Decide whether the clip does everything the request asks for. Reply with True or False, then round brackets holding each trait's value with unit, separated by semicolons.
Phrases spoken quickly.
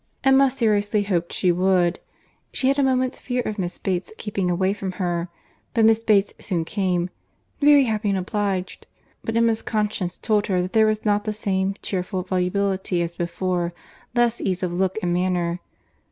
False (165 wpm)